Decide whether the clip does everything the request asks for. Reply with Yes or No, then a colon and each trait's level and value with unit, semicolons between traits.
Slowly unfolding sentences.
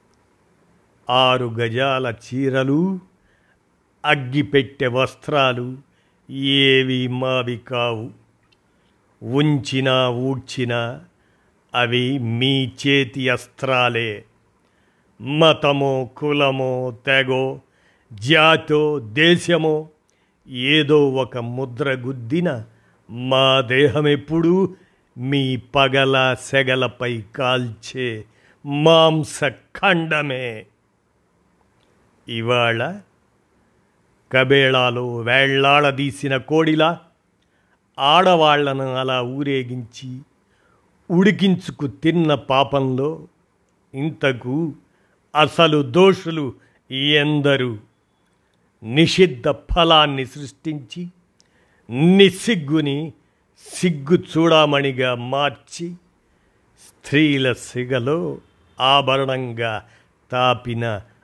Yes: slow, 55 wpm